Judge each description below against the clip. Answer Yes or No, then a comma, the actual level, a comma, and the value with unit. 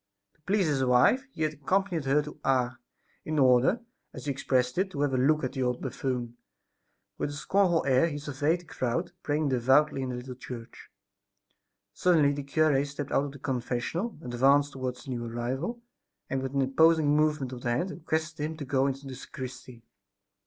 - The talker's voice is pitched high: No, medium, 140 Hz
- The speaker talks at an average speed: Yes, average, 195 wpm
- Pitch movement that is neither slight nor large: Yes, average, 3.3 semitones